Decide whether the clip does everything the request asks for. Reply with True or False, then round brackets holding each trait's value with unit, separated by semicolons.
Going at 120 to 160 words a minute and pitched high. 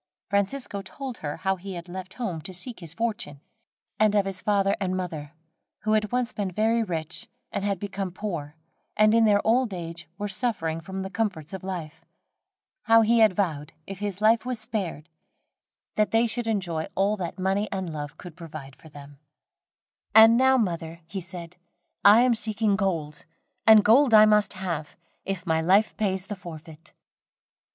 False (175 wpm; 195 Hz)